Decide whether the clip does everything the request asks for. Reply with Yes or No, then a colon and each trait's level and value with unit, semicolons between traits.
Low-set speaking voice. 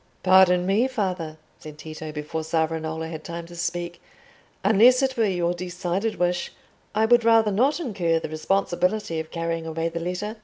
No: medium, 175 Hz